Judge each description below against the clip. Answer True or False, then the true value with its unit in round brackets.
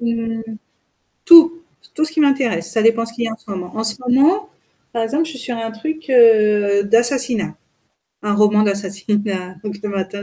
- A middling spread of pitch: True (3.7 semitones)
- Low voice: False (225 Hz)